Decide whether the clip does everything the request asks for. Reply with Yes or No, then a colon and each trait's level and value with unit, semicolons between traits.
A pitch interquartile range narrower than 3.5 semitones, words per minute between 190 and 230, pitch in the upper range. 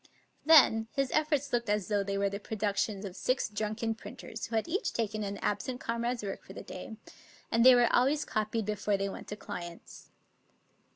Yes: average, 3.1 semitones; average, 195 wpm; high, 220 Hz